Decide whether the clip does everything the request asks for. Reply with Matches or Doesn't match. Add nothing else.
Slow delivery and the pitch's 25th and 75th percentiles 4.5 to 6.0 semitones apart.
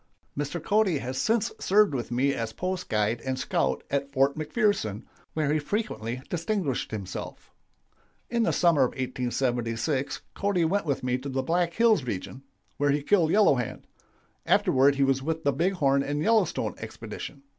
Doesn't match